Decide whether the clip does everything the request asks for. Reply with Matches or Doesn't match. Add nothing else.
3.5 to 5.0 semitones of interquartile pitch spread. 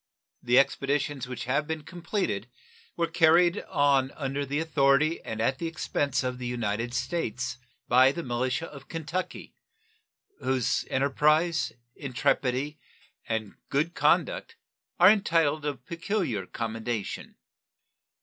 Matches